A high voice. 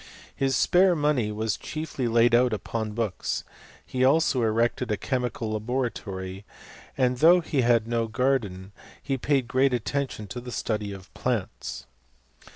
No: low, 120 Hz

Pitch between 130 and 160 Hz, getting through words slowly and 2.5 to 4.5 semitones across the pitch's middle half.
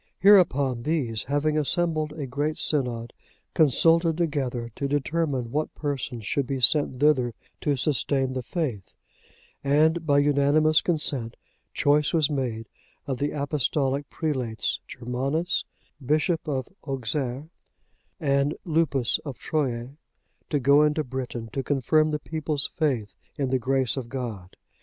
Yes: medium, 140 Hz; slow, 130 wpm; average, 3.2 semitones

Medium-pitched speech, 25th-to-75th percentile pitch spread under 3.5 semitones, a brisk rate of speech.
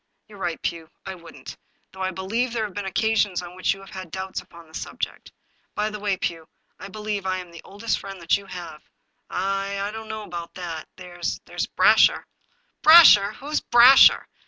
No: high, 195 Hz; average, 3.1 semitones; fast, 210 wpm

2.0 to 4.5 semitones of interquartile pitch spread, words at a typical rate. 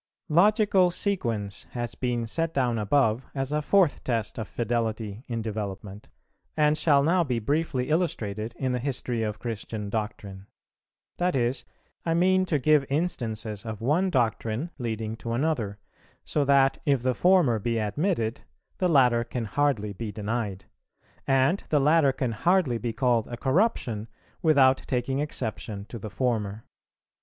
No: average, 5.3 semitones; average, 150 wpm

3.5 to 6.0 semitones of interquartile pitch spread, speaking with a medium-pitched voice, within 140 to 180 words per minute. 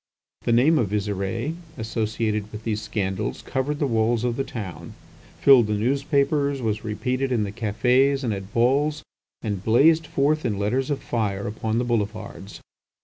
No: average, 4.3 semitones; low, 115 Hz; average, 160 wpm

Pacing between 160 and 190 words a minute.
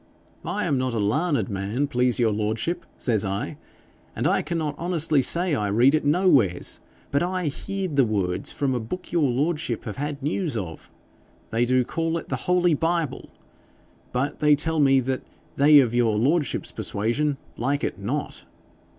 Yes: average, 170 wpm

